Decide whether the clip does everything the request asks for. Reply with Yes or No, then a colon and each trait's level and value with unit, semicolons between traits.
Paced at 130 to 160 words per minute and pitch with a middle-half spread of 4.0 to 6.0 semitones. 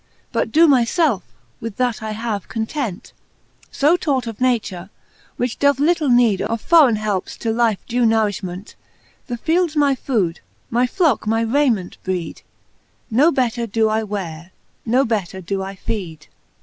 Yes: average, 155 wpm; average, 4.5 semitones